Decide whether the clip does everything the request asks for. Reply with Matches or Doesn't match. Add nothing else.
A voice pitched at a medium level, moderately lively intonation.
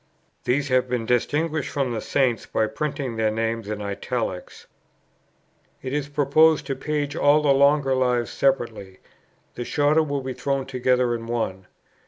Doesn't match